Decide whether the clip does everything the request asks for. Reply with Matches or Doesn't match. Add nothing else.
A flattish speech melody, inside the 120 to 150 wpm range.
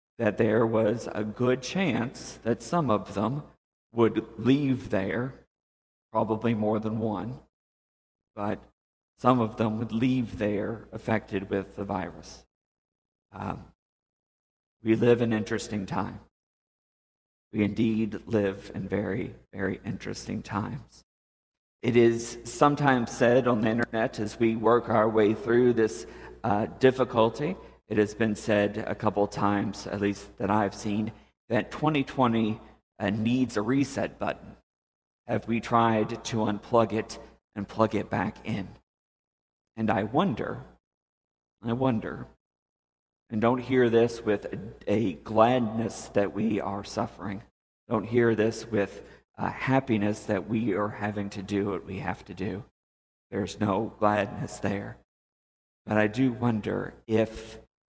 Matches